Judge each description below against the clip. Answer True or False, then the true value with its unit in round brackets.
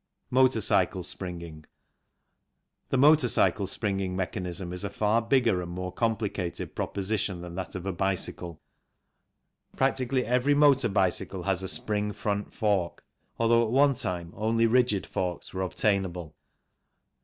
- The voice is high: False (100 Hz)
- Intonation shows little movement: False (4.1 semitones)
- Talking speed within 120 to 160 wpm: True (140 wpm)